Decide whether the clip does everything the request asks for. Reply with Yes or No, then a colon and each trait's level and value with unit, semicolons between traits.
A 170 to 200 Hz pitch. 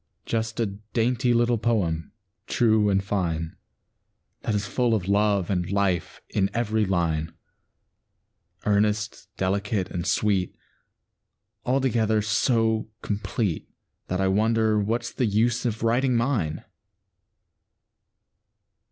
No: low, 105 Hz